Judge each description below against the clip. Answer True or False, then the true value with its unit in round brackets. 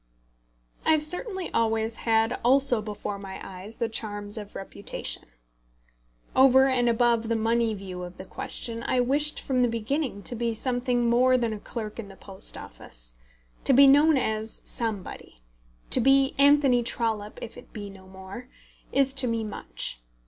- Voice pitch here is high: True (230 Hz)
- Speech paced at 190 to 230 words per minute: False (165 wpm)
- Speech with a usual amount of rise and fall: True (3.6 semitones)